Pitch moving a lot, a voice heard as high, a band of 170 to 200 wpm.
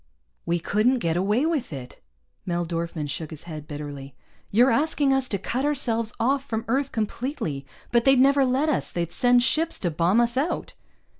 Yes: wide, 7.9 semitones; high, 230 Hz; average, 180 wpm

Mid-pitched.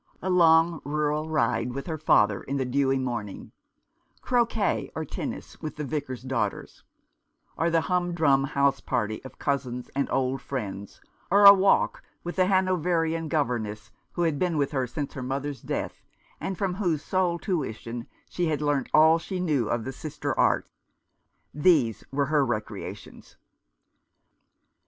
Yes: medium, 145 Hz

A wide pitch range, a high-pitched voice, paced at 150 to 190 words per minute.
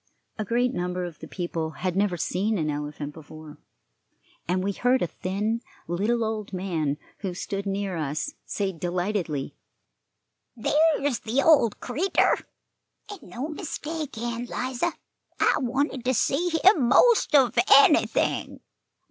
No: wide, 6.8 semitones; high, 215 Hz; slow, 135 wpm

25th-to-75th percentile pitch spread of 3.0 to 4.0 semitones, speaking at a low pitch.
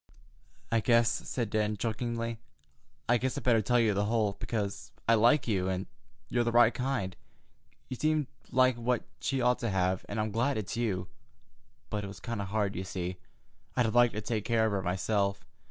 Yes: average, 3.3 semitones; low, 110 Hz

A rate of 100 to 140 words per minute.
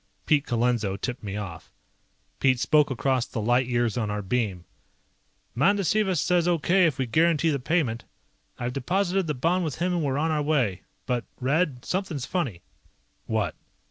No: average, 165 wpm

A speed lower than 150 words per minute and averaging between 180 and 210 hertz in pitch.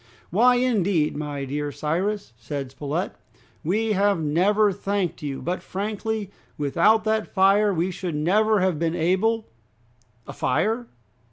Yes: average, 140 wpm; medium, 185 Hz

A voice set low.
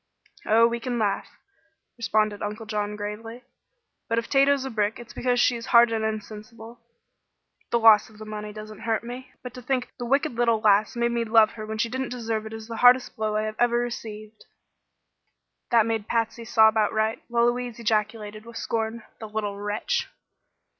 No: high, 225 Hz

